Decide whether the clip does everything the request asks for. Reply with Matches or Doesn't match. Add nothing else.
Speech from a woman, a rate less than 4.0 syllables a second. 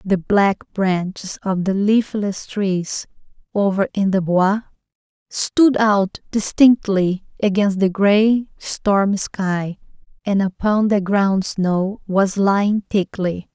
Matches